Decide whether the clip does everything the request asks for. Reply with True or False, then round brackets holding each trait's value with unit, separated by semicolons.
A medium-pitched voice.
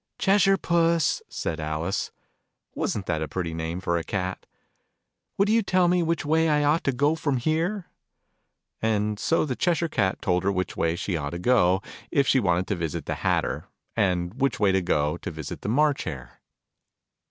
False (105 Hz)